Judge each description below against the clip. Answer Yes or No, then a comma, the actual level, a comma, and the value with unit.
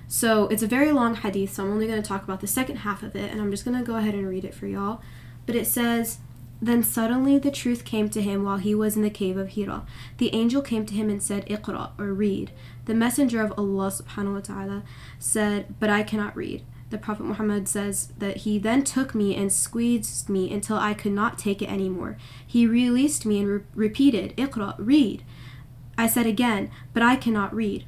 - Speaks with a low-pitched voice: No, high, 210 Hz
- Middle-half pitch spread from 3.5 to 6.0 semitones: No, average, 2.8 semitones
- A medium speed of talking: No, fast, 215 wpm